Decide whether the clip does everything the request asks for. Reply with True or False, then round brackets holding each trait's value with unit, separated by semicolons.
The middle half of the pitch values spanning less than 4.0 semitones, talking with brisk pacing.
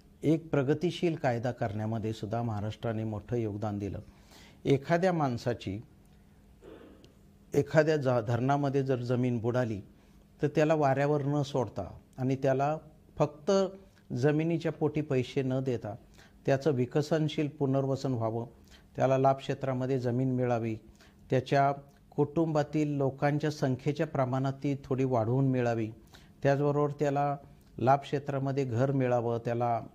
False (3.3 semitones; 105 wpm)